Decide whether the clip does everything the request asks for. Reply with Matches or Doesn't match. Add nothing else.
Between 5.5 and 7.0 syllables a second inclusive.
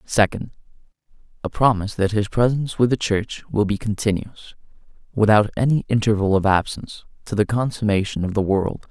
Matches